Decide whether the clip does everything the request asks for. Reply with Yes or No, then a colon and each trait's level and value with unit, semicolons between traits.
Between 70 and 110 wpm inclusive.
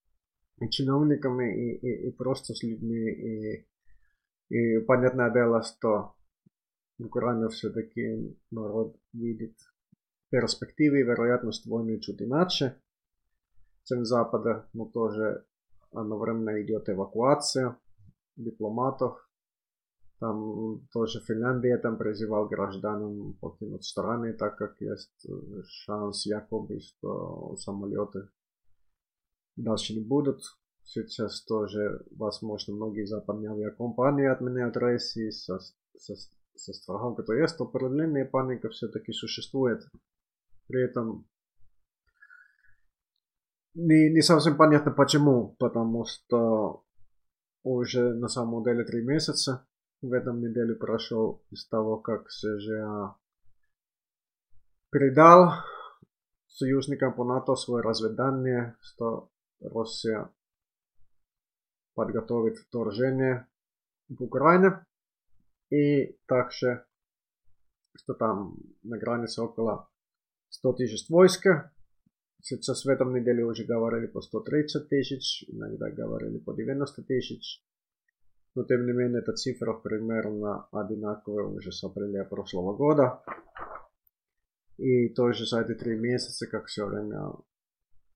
Yes: average, 100 wpm